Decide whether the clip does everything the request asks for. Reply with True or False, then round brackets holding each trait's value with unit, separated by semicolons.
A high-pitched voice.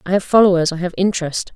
False (180 Hz)